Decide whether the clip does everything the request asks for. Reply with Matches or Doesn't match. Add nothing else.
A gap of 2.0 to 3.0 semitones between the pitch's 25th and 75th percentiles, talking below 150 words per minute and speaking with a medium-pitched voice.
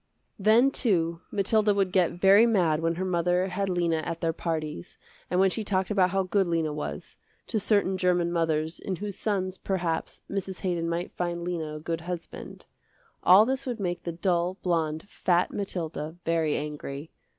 Doesn't match